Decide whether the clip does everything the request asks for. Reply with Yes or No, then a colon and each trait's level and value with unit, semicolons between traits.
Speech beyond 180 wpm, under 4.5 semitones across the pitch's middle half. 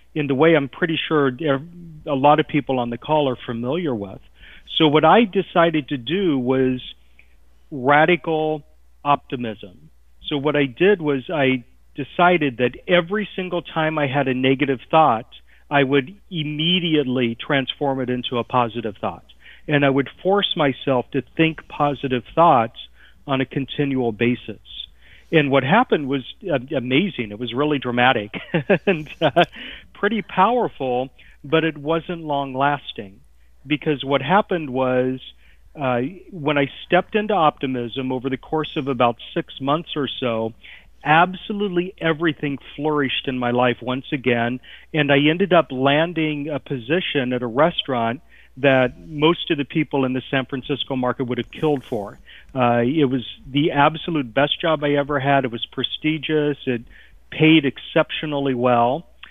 No: average, 150 wpm; average, 3.9 semitones